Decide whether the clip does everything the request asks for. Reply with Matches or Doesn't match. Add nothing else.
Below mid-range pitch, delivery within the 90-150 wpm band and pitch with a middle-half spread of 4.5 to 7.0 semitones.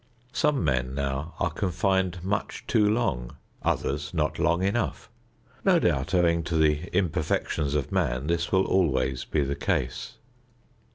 Matches